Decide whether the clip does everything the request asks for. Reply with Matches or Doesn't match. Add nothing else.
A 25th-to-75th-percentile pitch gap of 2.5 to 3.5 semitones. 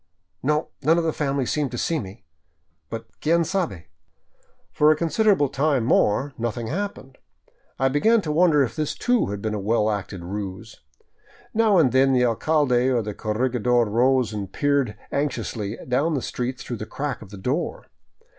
Doesn't match